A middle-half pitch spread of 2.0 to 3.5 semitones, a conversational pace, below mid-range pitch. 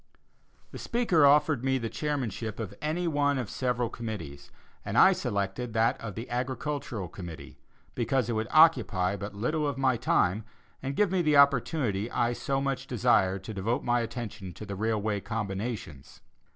No: average, 5.1 semitones; average, 165 wpm; low, 120 Hz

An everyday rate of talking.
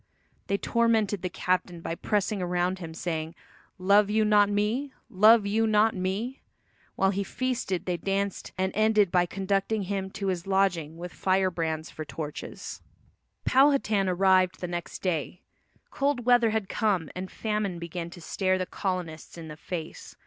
Yes: average, 160 wpm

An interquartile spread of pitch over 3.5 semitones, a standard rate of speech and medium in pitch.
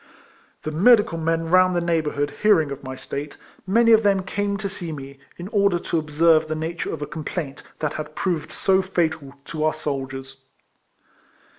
Yes: average, 4.0 semitones; average, 180 wpm; medium, 160 Hz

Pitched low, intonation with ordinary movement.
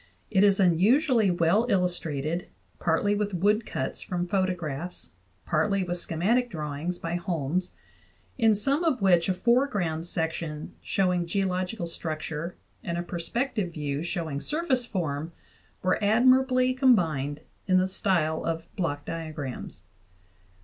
No: medium, 180 Hz; average, 4.2 semitones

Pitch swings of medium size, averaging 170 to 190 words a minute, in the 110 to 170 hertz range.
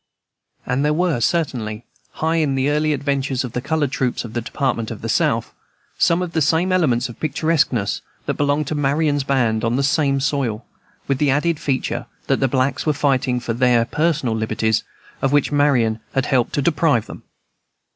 Yes: average, 3.5 semitones; average, 185 wpm; medium, 140 Hz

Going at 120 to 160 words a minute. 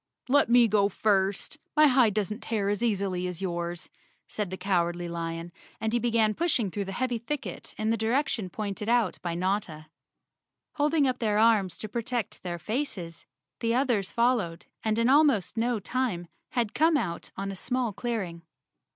No: average, 170 wpm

